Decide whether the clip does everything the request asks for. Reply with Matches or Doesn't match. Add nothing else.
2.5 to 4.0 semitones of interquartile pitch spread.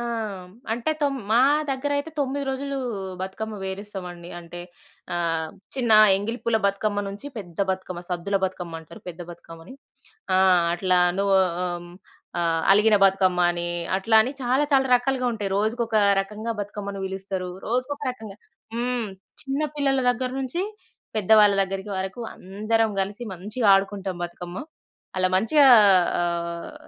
Doesn't match